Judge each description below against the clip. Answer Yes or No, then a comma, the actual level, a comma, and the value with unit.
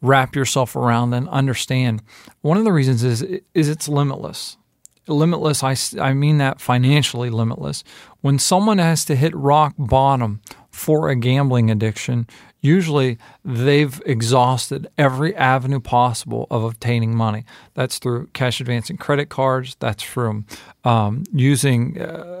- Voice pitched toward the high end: No, low, 135 Hz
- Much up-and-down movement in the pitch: No, average, 3.3 semitones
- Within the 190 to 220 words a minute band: No, slow, 135 wpm